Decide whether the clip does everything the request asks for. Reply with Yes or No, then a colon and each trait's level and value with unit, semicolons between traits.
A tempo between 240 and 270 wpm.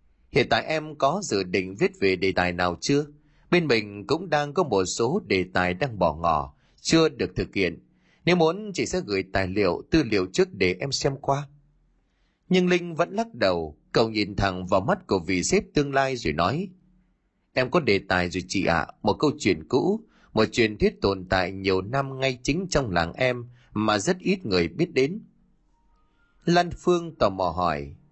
No: average, 200 wpm